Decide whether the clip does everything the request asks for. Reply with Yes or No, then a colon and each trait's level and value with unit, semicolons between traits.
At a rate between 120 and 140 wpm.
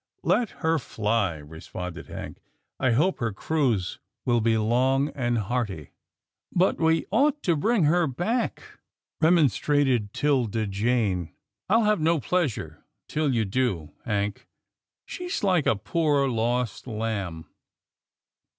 Yes: slow, 135 wpm